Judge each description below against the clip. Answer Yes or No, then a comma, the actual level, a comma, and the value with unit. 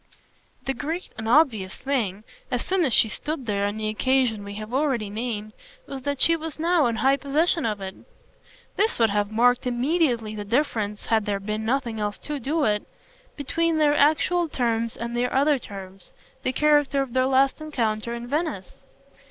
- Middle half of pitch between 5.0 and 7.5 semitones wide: Yes, average, 5.3 semitones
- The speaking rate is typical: Yes, average, 185 wpm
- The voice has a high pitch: Yes, high, 245 Hz